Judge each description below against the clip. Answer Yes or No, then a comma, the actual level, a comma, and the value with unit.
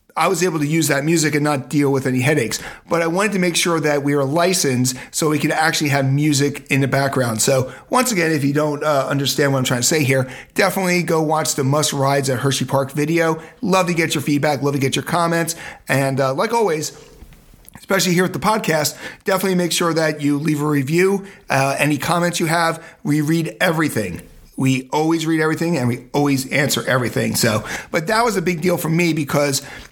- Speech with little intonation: No, average, 3.5 semitones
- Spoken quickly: Yes, fast, 220 wpm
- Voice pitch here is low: No, medium, 150 Hz